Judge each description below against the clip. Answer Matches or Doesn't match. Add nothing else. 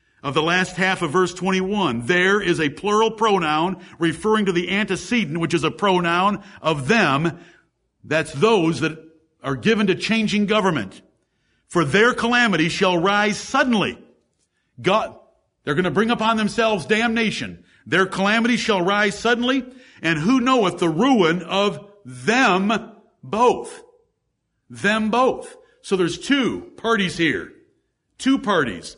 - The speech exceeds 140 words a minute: Doesn't match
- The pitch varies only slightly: Doesn't match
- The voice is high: Matches